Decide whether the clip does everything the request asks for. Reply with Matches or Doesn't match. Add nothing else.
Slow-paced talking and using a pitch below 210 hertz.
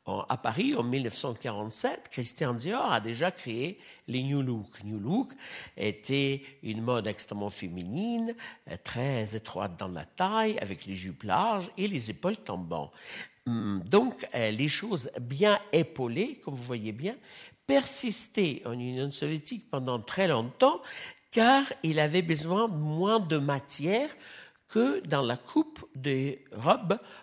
Matches